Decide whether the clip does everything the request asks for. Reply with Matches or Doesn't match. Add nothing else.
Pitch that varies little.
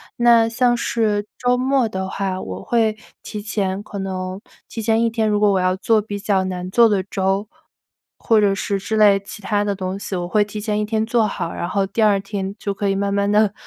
Matches